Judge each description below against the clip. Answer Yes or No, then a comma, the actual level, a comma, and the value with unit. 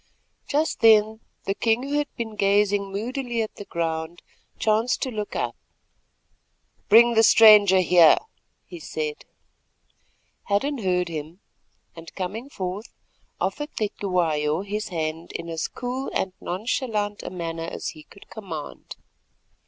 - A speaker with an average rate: No, slow, 130 wpm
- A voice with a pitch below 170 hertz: No, high, 200 Hz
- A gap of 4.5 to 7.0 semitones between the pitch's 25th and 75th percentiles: Yes, average, 4.8 semitones